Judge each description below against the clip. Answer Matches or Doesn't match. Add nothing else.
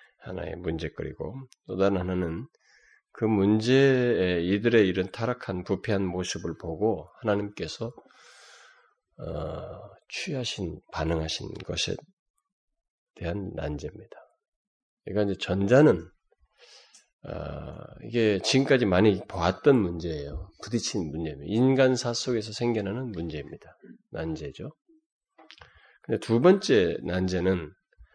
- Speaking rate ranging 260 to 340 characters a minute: Doesn't match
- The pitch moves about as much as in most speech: Doesn't match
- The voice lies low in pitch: Matches